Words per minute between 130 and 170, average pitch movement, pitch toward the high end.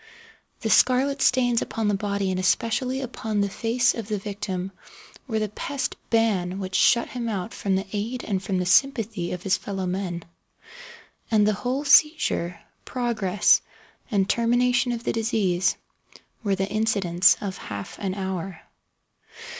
Yes: average, 155 wpm; average, 3.7 semitones; high, 210 Hz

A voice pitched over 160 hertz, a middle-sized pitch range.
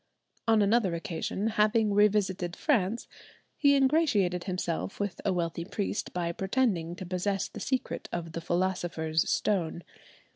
Yes: high, 190 Hz; average, 3.6 semitones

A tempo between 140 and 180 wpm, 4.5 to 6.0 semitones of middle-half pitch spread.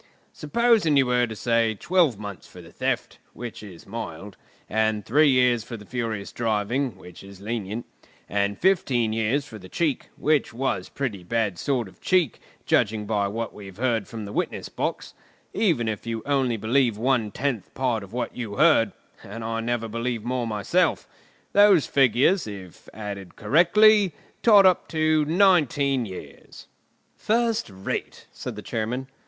Yes: average, 160 wpm; average, 5.1 semitones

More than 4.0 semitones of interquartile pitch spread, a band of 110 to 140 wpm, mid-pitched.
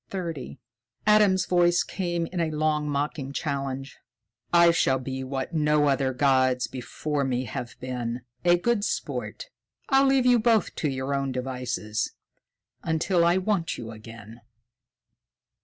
Yes: average, 5.0 semitones; slow, 135 wpm; medium, 145 Hz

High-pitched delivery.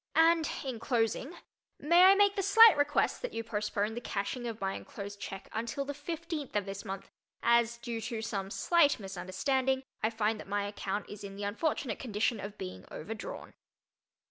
Yes: high, 230 Hz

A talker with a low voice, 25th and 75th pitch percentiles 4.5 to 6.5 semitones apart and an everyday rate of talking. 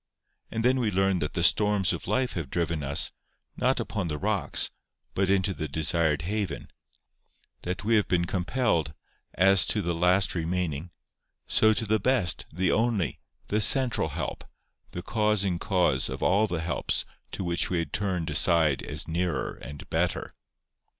No: very low, 90 Hz; average, 3.9 semitones; average, 165 wpm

